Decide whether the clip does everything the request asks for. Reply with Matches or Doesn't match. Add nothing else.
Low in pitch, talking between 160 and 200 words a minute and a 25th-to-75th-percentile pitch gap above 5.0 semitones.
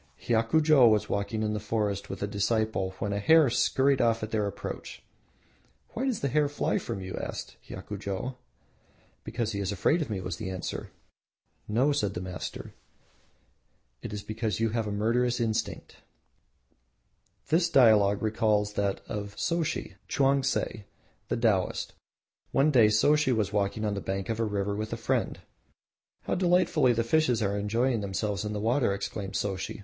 Doesn't match